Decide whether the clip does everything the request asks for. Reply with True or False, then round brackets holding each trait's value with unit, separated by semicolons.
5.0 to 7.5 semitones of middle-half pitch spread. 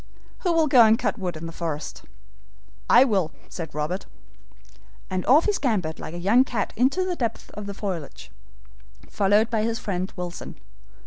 True (5.5 semitones)